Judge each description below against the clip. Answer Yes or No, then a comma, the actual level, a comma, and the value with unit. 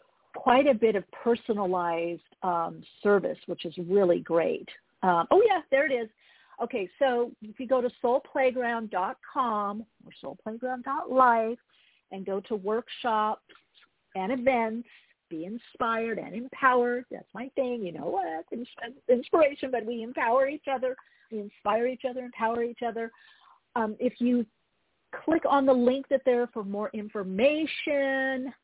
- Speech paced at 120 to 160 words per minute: Yes, average, 140 wpm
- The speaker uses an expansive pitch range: No, average, 3.8 semitones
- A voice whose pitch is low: No, high, 240 Hz